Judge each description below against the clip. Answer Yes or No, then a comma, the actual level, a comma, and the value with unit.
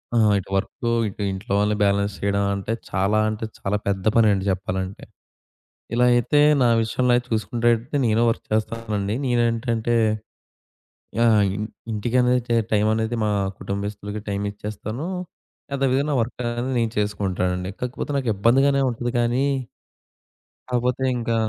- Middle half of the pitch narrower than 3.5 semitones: Yes, average, 3.0 semitones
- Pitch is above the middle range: No, low, 110 Hz